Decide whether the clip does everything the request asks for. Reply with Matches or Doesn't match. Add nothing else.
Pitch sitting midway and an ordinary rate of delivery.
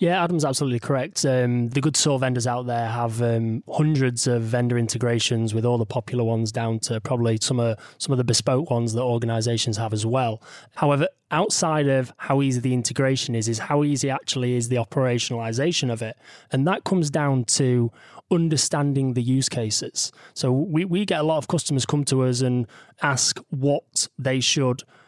Doesn't match